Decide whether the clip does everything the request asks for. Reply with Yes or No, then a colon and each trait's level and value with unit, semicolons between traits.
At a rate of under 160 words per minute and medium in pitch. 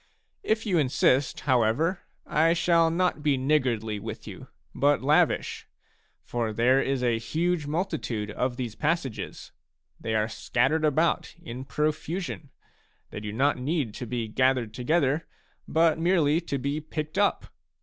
Yes: average, 150 wpm; medium, 145 Hz